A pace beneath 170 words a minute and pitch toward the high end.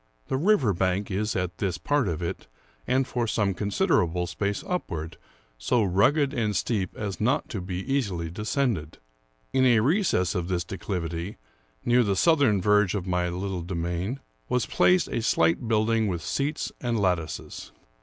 No: average, 160 wpm; low, 100 Hz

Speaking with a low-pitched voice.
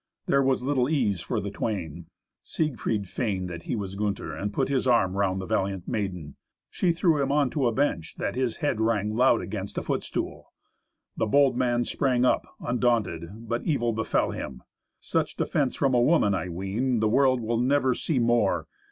Yes: low, 115 Hz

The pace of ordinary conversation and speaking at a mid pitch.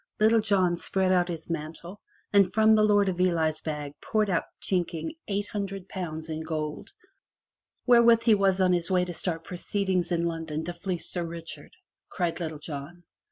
Yes: average, 175 wpm; medium, 175 Hz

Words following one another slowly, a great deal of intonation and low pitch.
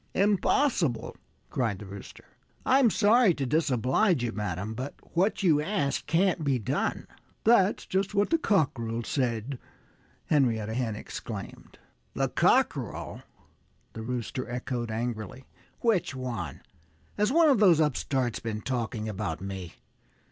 Yes: slow, 125 wpm; wide, 9.0 semitones; low, 130 Hz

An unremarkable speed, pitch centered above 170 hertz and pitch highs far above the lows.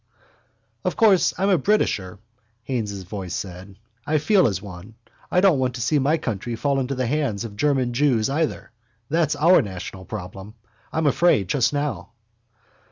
No: average, 170 wpm; low, 125 Hz; wide, 6.9 semitones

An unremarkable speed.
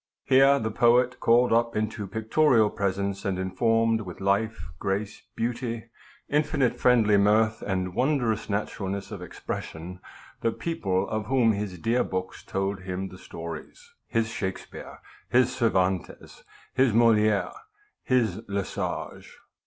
No: slow, 130 wpm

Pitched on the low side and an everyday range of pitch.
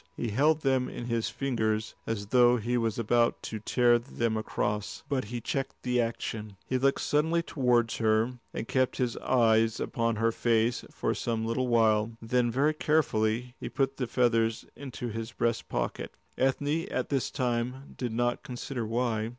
No: low, 120 Hz; narrow, 2.3 semitones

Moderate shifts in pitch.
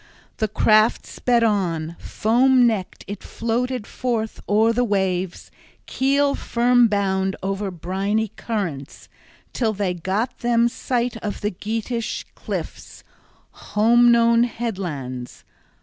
Yes: average, 3.7 semitones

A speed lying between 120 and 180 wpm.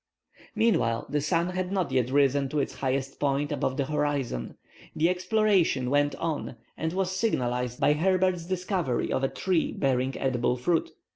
Yes: average, 160 wpm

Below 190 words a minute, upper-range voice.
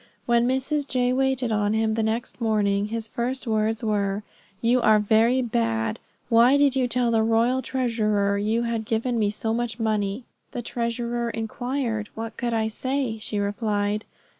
Yes: average, 165 wpm; high, 225 Hz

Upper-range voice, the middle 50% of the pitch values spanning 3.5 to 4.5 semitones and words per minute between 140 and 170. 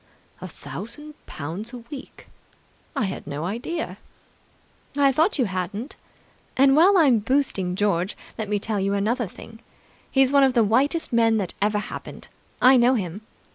No: high, 230 Hz; average, 5.1 semitones; average, 160 wpm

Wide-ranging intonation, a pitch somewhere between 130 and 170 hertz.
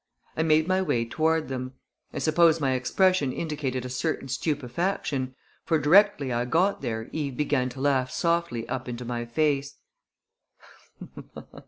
No: average, 4.2 semitones; medium, 140 Hz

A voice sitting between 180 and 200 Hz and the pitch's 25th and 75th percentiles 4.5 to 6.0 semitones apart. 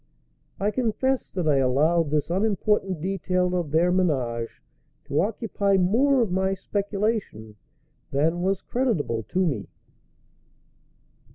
Yes: medium, 185 Hz; average, 5.1 semitones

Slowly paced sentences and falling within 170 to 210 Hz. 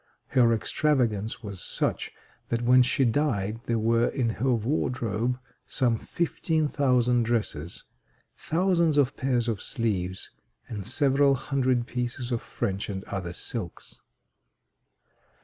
No: slow, 120 wpm; low, 120 Hz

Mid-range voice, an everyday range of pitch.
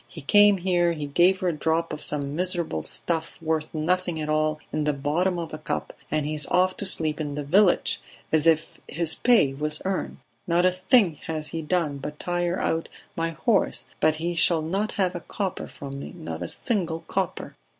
Yes: medium, 165 Hz; average, 3.0 semitones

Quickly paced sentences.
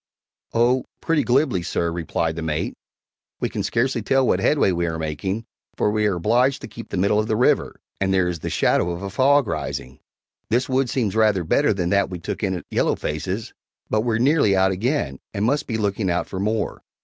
Yes: fast, 215 wpm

